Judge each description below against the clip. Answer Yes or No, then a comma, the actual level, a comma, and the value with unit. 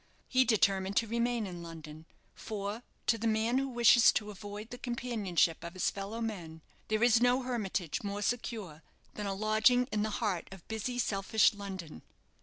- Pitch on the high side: Yes, high, 215 Hz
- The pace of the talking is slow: No, average, 175 wpm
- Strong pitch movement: No, average, 3.6 semitones